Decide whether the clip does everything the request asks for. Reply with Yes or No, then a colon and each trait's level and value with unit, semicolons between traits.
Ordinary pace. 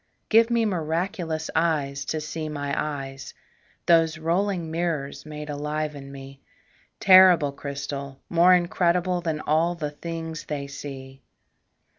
No: slow, 125 wpm